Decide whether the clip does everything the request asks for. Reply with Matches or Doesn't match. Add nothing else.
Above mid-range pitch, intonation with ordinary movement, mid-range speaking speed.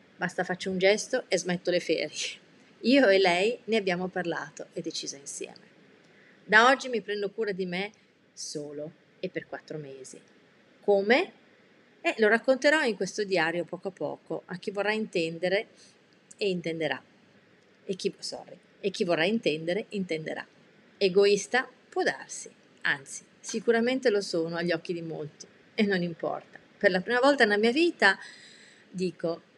Matches